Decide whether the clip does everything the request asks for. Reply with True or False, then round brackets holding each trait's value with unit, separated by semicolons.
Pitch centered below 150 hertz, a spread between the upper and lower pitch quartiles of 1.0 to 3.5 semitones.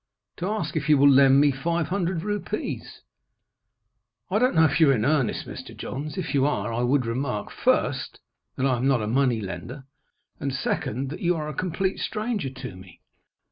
False (140 Hz; 4.8 semitones)